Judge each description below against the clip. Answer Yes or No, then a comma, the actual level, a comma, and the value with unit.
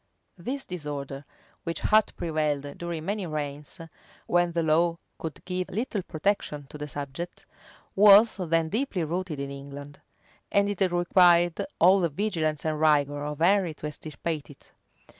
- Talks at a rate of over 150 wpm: No, average, 145 wpm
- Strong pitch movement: No, average, 3.7 semitones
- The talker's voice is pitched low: No, medium, 165 Hz